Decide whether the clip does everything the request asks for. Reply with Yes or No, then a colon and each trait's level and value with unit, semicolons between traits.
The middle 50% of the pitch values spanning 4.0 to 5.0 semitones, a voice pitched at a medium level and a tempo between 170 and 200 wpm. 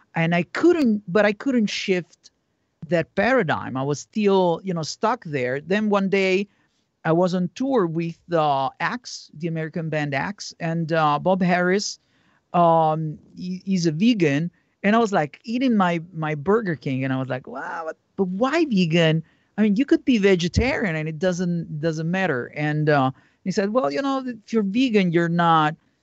Yes: average, 4.4 semitones; medium, 175 Hz; average, 185 wpm